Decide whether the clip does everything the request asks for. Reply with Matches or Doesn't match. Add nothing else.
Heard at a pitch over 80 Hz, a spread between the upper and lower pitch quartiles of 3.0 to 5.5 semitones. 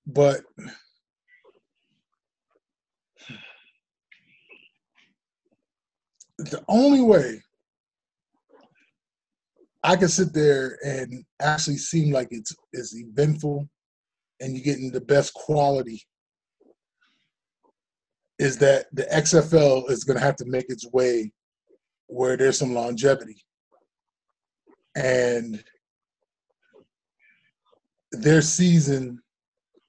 Matches